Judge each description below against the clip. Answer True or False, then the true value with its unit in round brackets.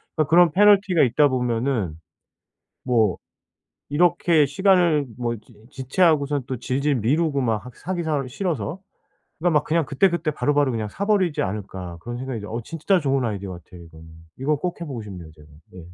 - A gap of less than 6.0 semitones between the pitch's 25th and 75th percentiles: False (6.4 semitones)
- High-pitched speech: False (140 Hz)